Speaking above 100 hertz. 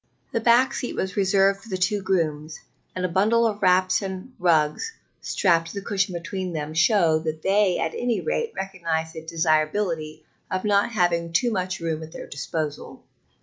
Yes: medium, 185 Hz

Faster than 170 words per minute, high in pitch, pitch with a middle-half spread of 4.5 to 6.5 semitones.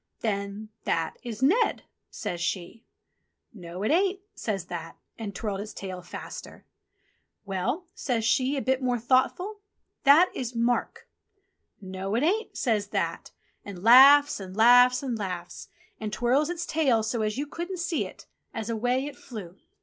No: average, 155 wpm; high, 235 Hz; wide, 5.6 semitones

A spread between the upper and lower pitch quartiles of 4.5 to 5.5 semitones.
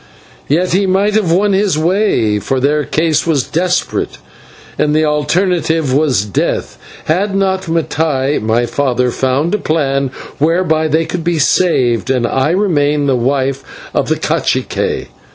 Yes: average, 4.8 semitones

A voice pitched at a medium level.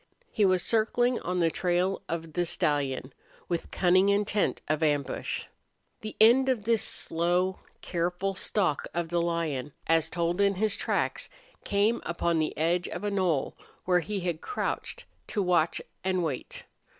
Yes: medium, 180 Hz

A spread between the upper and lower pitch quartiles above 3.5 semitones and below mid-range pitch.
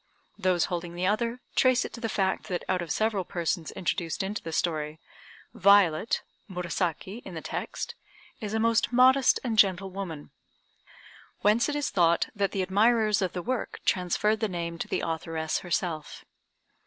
No: average, 4.2 semitones; high, 190 Hz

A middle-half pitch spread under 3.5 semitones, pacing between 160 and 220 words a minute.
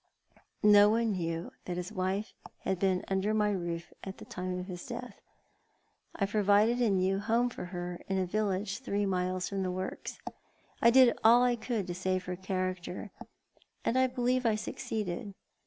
Yes: average, 3.1 semitones; average, 175 wpm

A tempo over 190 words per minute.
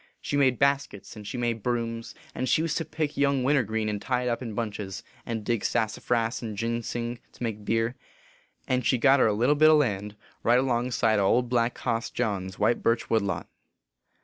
Yes: fast, 205 wpm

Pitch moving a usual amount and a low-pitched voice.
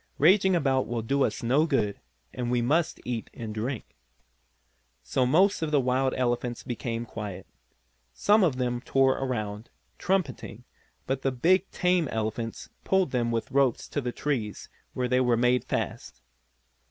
Yes: average, 3.6 semitones; low, 125 Hz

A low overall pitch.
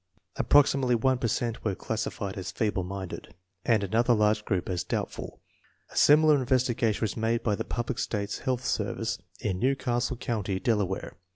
Yes: low, 115 Hz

